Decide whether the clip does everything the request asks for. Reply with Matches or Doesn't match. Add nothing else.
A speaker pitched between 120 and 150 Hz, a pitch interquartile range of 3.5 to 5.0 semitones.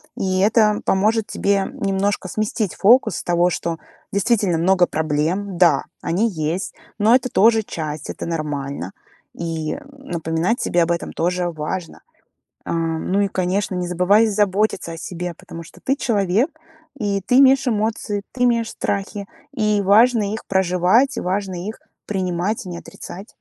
Doesn't match